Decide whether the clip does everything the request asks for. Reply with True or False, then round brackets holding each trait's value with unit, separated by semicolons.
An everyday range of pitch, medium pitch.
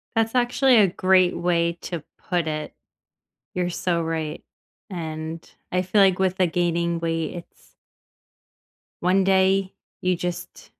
False (2.2 semitones; 180 Hz)